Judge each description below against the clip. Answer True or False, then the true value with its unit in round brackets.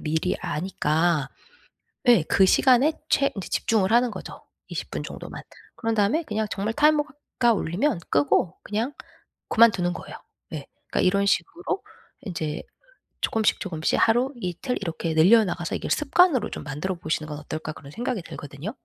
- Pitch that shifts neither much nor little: False (6.8 semitones)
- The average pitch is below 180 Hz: False (195 Hz)